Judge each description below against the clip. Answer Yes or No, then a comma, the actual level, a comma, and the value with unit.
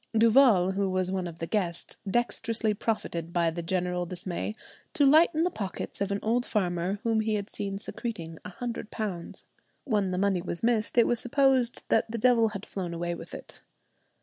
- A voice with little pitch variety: No, average, 4.4 semitones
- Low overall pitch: No, high, 200 Hz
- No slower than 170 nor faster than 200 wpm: Yes, average, 190 wpm